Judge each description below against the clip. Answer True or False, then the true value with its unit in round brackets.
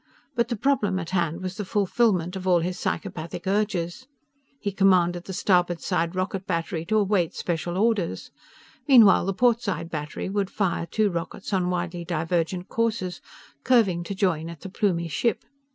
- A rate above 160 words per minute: True (170 wpm)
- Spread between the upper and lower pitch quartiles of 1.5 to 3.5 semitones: True (3.2 semitones)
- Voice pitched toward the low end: False (185 Hz)